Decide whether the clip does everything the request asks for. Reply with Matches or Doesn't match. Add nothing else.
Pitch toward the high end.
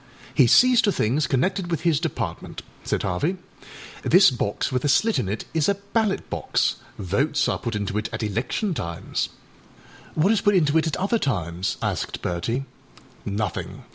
Doesn't match